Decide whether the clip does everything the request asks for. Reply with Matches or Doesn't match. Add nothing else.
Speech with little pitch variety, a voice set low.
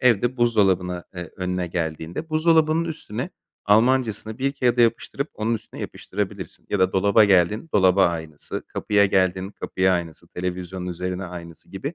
Doesn't match